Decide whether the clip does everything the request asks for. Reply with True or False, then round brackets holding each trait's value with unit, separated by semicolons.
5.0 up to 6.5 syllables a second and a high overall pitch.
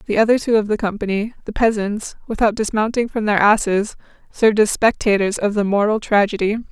True (5.8 syllables/s; 210 Hz)